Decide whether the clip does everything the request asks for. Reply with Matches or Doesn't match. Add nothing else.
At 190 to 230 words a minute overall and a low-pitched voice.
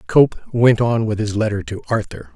Matches